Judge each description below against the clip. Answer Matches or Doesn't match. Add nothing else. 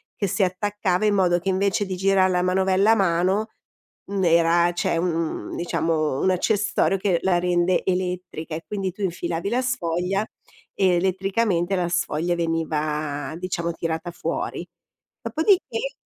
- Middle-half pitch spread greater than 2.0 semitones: Matches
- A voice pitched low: Doesn't match